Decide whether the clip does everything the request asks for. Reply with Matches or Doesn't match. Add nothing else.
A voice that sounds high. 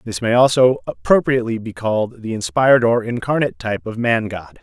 Doesn't match